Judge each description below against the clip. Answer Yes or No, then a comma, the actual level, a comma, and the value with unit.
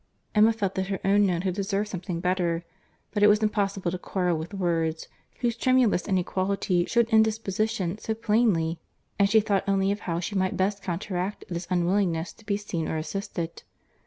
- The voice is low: No, high, 195 Hz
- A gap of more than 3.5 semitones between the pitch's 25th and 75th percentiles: No, average, 3.0 semitones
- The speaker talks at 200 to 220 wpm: No, average, 180 wpm